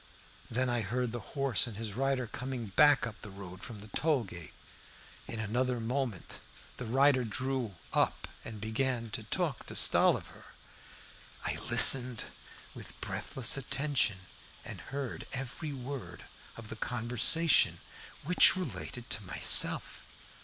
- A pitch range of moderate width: Yes, average, 3.4 semitones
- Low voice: Yes, low, 125 Hz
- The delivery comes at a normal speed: No, slow, 130 wpm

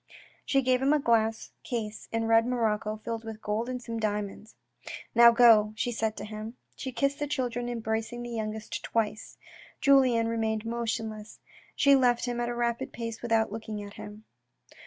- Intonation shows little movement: Yes, narrow, 1.8 semitones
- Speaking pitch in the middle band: No, high, 230 Hz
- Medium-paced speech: Yes, average, 180 wpm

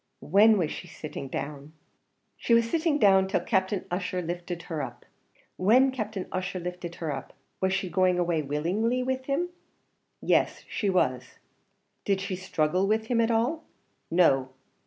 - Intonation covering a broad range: No, average, 4.7 semitones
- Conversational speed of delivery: Yes, average, 155 wpm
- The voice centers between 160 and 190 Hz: Yes, medium, 185 Hz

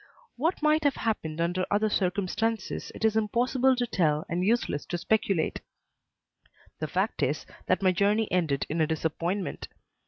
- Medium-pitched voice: No, high, 200 Hz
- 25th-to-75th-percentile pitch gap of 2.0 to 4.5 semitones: No, average, 5.1 semitones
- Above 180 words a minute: No, average, 155 wpm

